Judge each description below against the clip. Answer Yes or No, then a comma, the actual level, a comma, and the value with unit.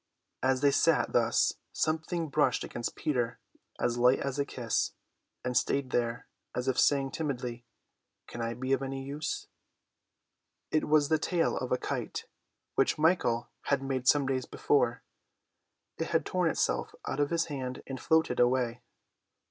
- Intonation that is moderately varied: Yes, average, 3.0 semitones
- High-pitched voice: No, low, 135 Hz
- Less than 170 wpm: Yes, average, 155 wpm